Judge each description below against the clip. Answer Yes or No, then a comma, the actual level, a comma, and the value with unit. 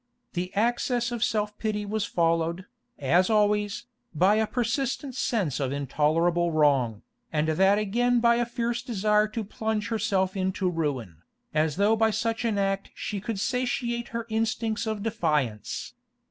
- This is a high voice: Yes, high, 210 Hz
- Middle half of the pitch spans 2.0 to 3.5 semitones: No, average, 5.1 semitones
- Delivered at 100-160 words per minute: Yes, average, 145 wpm